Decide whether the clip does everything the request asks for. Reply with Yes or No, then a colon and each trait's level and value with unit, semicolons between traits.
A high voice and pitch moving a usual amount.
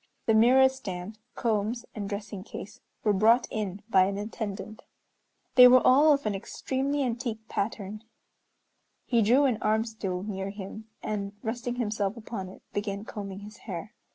Yes: high, 215 Hz; average, 3.0 semitones